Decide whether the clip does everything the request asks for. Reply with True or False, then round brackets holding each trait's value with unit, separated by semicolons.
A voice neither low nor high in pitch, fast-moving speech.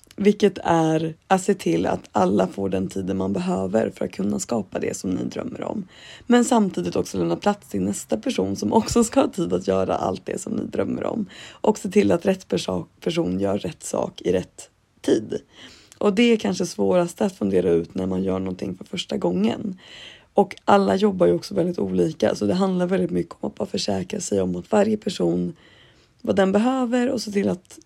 True (170 Hz; 210 wpm)